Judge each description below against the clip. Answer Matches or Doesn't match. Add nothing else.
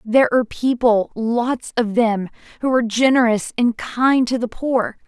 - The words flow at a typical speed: Matches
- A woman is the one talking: Matches